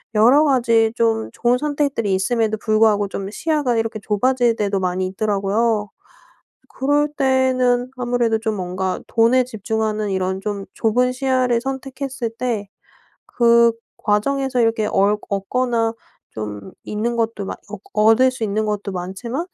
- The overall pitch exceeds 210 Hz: Yes, high, 225 Hz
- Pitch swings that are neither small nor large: Yes, average, 3.3 semitones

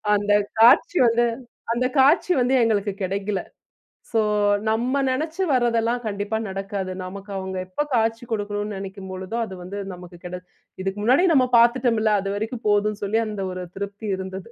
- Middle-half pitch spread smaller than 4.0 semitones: Yes, average, 3.3 semitones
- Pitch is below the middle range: No, high, 210 Hz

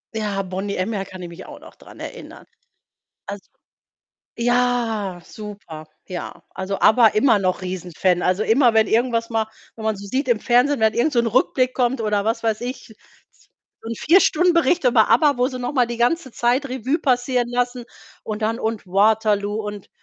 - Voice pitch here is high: Yes, high, 225 Hz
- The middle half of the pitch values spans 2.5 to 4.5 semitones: Yes, average, 3.4 semitones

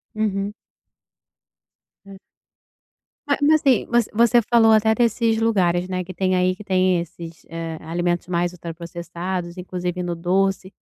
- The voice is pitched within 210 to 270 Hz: No, medium, 185 Hz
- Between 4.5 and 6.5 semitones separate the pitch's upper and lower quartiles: No, average, 3.8 semitones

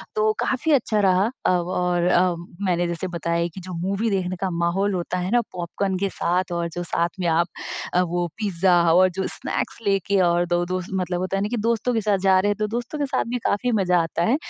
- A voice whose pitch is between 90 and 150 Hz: No, medium, 185 Hz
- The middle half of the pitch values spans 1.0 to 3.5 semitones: Yes, average, 2.8 semitones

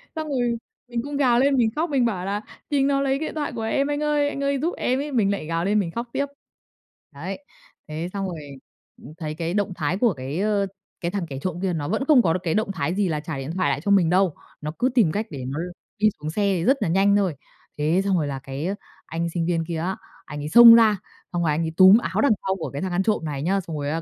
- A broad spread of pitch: Yes, wide, 6.5 semitones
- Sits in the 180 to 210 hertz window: Yes, high, 190 Hz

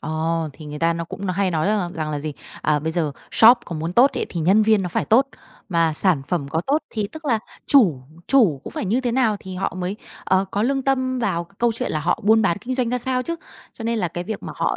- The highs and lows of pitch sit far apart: Yes, wide, 6.1 semitones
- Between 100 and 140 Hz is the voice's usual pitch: No, high, 190 Hz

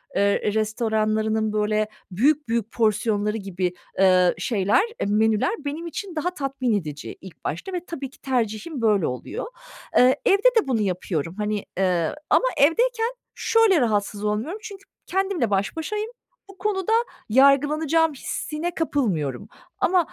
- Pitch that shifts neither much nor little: No, wide, 8.0 semitones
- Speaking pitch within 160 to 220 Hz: No, high, 235 Hz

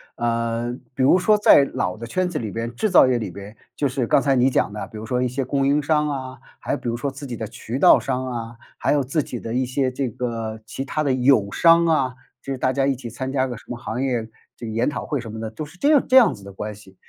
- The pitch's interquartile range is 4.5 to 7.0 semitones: No, average, 3.3 semitones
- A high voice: No, low, 125 Hz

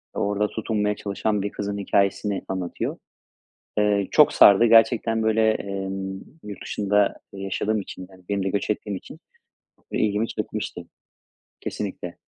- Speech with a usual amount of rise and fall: No, narrow, 1.5 semitones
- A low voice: Yes, low, 100 Hz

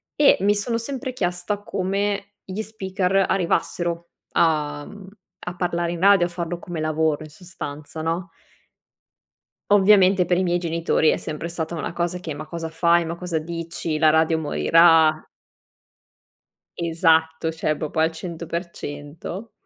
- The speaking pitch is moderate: Yes, medium, 170 Hz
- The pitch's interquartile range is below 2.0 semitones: No, average, 2.7 semitones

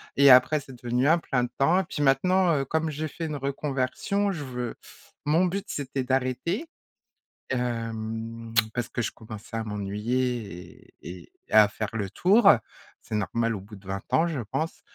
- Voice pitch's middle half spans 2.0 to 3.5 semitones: No, average, 5.2 semitones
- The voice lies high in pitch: No, low, 130 Hz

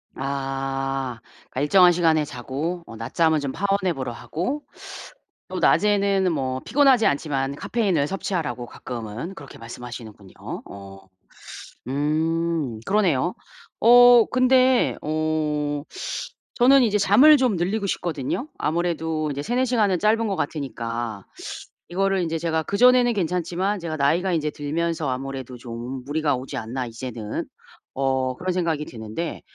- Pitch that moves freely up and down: Yes, wide, 6.5 semitones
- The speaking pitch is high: No, medium, 155 Hz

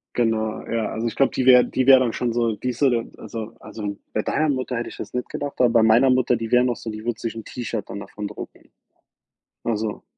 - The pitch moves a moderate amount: No, narrow, 2.1 semitones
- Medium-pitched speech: No, low, 115 Hz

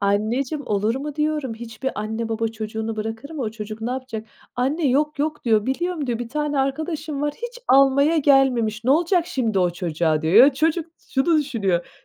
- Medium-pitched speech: No, very high, 260 Hz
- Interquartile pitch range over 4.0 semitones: Yes, average, 5.2 semitones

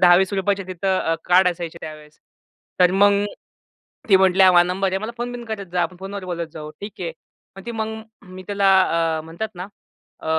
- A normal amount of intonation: No, narrow, 2.3 semitones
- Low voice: No, medium, 185 Hz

